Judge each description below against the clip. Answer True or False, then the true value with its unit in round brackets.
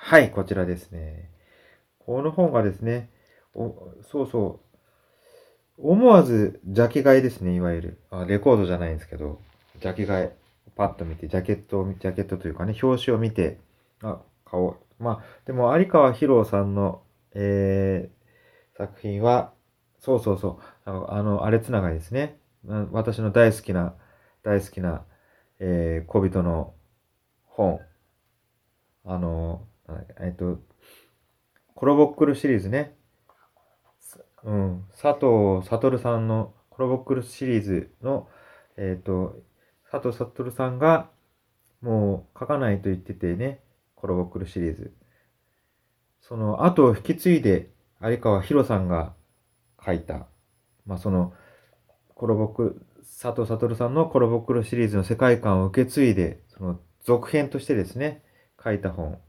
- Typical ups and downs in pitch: True (4.6 semitones)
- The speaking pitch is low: True (105 Hz)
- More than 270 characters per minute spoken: False (260 characters per minute)